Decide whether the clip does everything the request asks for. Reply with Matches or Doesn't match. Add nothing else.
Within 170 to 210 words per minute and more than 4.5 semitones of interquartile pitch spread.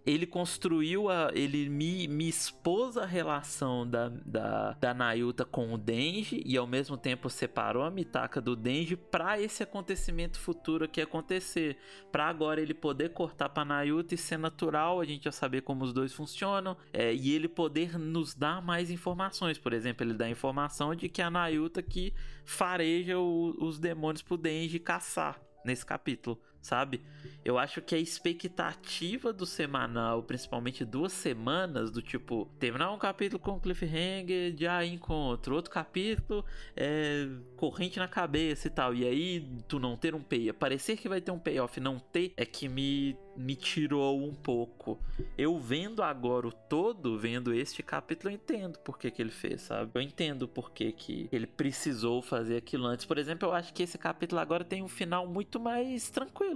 Matches